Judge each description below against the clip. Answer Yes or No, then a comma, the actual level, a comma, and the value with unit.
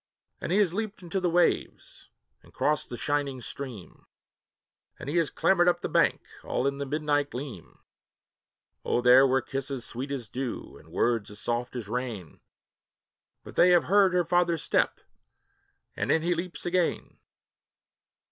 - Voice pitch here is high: No, medium, 140 Hz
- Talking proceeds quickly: No, average, 160 wpm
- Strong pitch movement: Yes, wide, 5.9 semitones